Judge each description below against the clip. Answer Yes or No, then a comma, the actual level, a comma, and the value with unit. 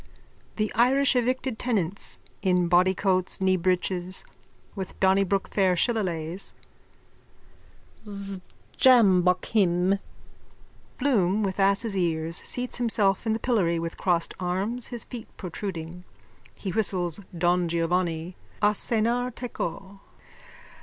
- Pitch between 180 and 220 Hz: Yes, high, 190 Hz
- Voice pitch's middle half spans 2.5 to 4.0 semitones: Yes, average, 3.6 semitones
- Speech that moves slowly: Yes, slow, 100 wpm